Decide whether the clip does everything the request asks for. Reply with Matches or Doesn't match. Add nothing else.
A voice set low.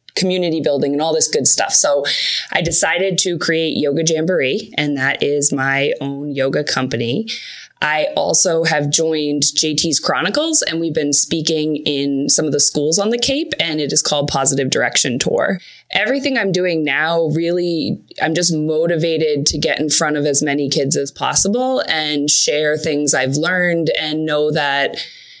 Doesn't match